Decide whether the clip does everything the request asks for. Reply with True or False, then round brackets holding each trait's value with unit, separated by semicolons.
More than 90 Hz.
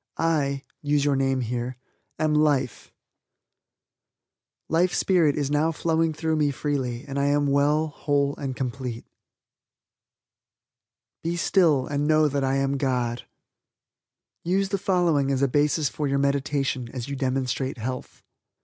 True (140 Hz)